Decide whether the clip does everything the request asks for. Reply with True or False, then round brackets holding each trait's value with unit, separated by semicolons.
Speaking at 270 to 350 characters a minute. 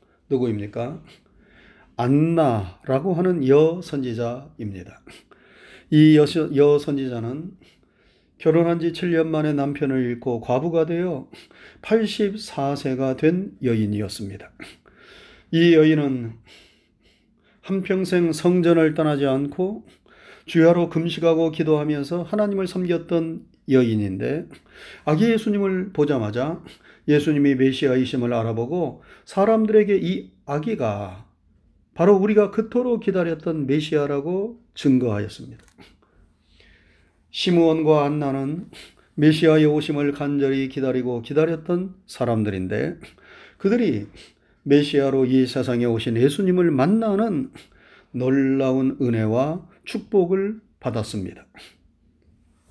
False (240 characters per minute)